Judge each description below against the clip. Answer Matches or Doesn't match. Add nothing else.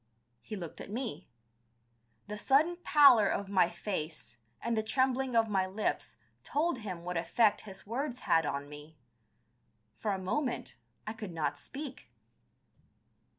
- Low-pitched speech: Doesn't match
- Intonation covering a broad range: Matches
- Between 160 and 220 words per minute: Doesn't match